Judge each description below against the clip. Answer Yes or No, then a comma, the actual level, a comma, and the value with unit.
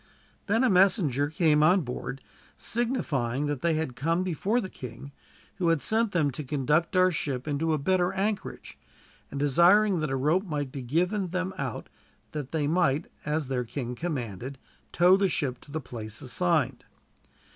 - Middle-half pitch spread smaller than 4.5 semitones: No, average, 5.2 semitones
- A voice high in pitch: No, medium, 155 Hz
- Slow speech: No, average, 170 wpm